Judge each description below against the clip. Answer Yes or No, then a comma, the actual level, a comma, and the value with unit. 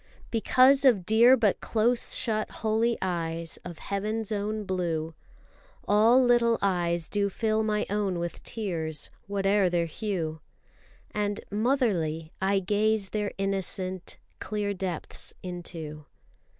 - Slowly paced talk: Yes, slow, 120 wpm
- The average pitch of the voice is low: No, high, 200 Hz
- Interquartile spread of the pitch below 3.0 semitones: No, average, 3.8 semitones